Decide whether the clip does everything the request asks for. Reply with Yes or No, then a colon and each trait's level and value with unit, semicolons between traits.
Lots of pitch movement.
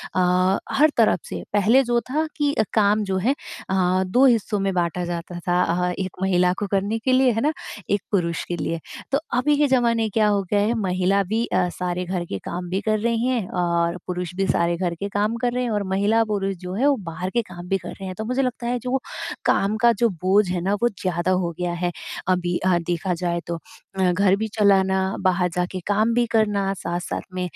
No: average, 3.8 semitones